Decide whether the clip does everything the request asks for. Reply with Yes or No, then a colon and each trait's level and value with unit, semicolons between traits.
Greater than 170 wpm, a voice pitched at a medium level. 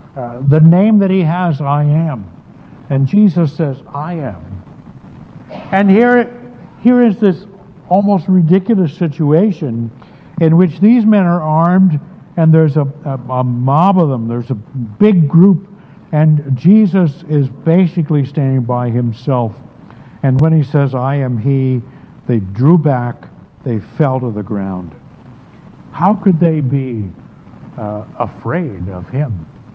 No: average, 140 wpm; medium, 150 Hz